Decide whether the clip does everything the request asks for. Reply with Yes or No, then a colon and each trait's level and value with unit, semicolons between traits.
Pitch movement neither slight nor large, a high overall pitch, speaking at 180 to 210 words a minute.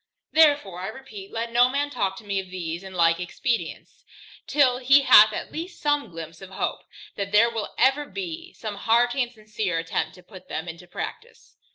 No: wide, 6.3 semitones; high, 215 Hz; average, 200 wpm